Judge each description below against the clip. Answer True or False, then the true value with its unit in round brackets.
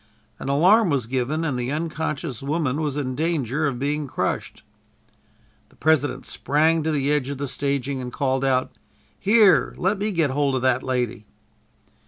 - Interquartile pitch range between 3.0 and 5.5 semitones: True (3.3 semitones)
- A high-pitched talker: False (140 Hz)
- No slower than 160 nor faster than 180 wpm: True (170 wpm)